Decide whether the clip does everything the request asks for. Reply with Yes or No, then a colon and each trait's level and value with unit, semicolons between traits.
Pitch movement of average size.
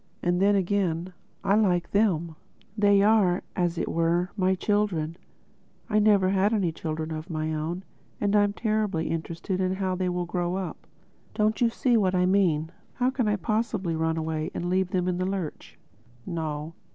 Yes: average, 3.5 semitones